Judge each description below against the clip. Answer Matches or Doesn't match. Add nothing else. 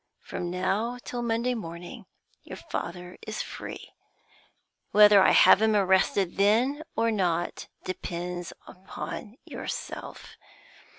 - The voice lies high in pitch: Matches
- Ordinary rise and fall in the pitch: Matches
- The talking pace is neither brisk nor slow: Doesn't match